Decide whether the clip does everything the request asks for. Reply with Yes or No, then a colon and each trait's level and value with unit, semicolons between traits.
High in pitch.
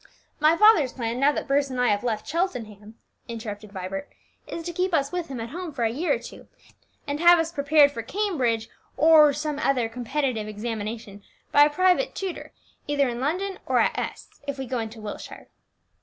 Yes: very high, 275 Hz